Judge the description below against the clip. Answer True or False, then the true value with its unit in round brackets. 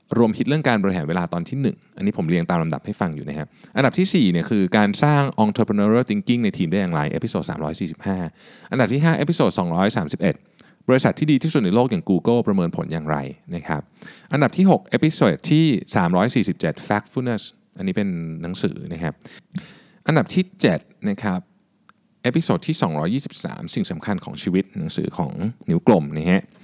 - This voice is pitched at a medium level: False (125 Hz)